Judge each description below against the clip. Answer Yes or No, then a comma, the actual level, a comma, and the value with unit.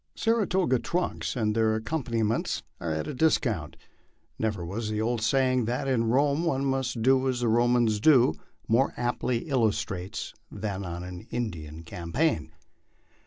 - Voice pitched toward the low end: Yes, low, 115 Hz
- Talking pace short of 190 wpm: Yes, average, 140 wpm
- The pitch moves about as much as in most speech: Yes, average, 4.0 semitones